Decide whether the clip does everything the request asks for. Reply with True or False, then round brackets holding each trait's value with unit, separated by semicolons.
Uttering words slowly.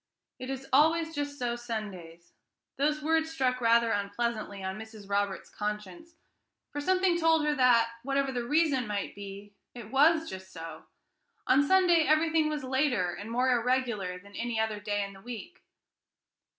False (160 wpm)